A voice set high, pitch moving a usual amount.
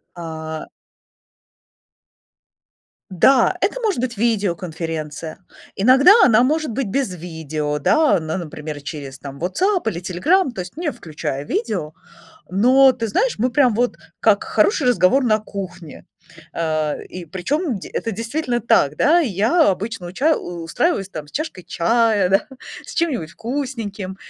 No: high, 200 Hz; wide, 7.5 semitones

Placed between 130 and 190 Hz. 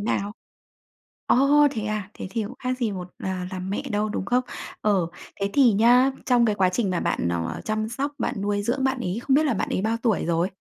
No: high, 215 Hz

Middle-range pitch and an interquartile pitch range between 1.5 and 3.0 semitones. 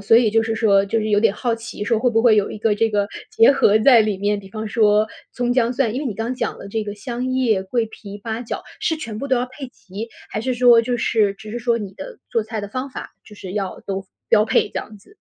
No: high, 225 Hz; average, 2.7 semitones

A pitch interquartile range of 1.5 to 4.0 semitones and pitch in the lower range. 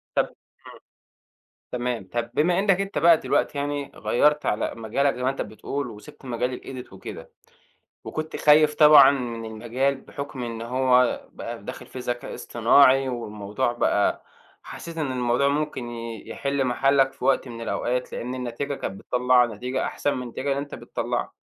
Yes: average, 3.0 semitones; low, 125 Hz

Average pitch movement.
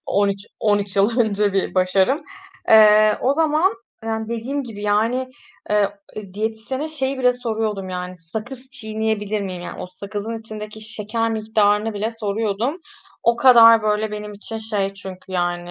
No: narrow, 2.2 semitones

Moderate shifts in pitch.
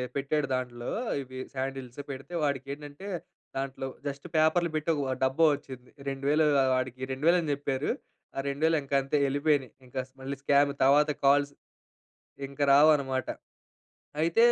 No: narrow, 2.0 semitones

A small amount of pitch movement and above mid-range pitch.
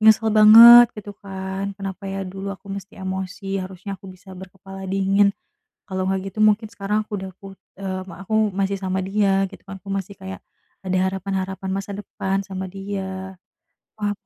Yes: narrow, 1.0 semitones; high, 195 Hz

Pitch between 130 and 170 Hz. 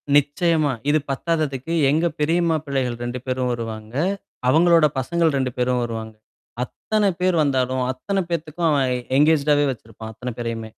Yes: medium, 140 Hz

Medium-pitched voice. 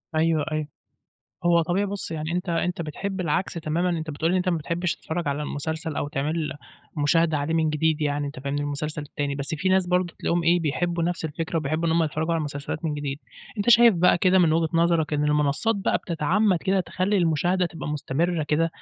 Yes: medium, 165 Hz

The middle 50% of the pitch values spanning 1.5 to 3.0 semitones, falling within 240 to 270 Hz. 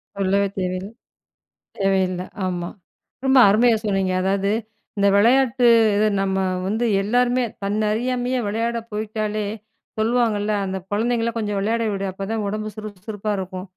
No: average, 2.7 semitones; high, 210 Hz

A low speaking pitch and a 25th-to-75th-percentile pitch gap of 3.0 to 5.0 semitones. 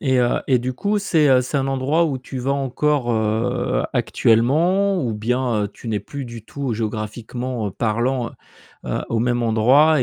Yes: low, 125 Hz; average, 3.4 semitones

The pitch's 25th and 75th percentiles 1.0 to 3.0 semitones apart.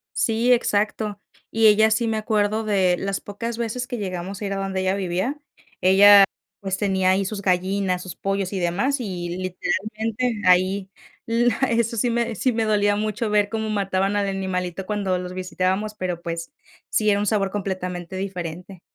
Yes: narrow, 2.6 semitones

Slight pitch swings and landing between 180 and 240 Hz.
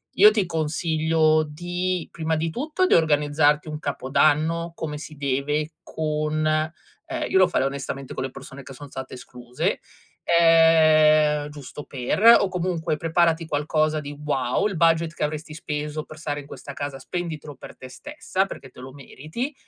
No: narrow, 2.3 semitones; medium, 155 Hz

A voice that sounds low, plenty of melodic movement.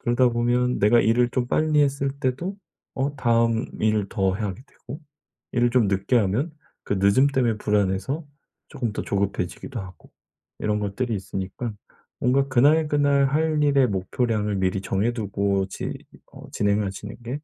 No: low, 120 Hz; average, 4.8 semitones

